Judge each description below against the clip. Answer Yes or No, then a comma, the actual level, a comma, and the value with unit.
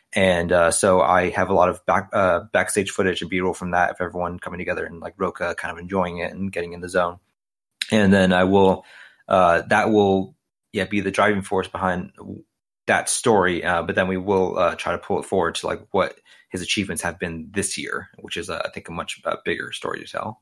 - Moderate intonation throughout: No, narrow, 1.6 semitones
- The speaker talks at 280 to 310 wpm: No, fast, 230 wpm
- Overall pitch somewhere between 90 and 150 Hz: Yes, very low, 95 Hz